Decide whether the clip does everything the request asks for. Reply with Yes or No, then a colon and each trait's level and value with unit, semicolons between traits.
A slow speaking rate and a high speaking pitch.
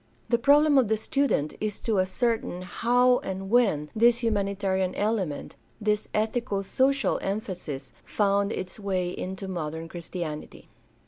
Yes: slow, 130 wpm; high, 200 Hz